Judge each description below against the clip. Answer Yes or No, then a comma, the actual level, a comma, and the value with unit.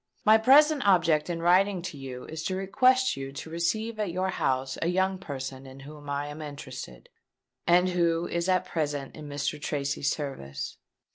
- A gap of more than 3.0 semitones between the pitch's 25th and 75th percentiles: Yes, average, 4.8 semitones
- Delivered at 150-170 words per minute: No, average, 180 wpm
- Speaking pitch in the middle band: Yes, medium, 165 Hz